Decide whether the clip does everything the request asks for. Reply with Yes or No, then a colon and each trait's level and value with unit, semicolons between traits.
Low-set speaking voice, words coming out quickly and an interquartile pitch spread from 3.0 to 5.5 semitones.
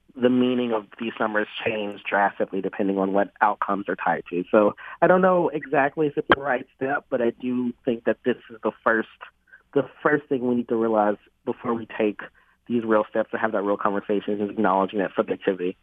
Yes: low, 110 Hz; fast, 210 wpm; average, 3.6 semitones